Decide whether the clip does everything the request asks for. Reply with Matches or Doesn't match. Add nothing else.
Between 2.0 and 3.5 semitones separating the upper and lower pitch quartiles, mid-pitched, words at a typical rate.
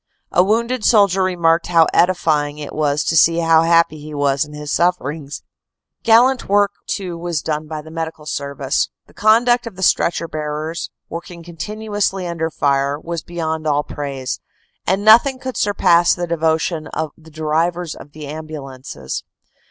Matches